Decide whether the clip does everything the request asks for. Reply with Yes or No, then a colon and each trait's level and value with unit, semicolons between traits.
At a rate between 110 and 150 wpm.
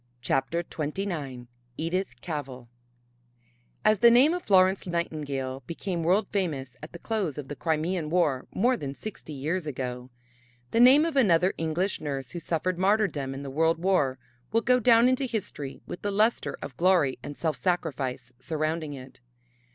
No: average, 160 wpm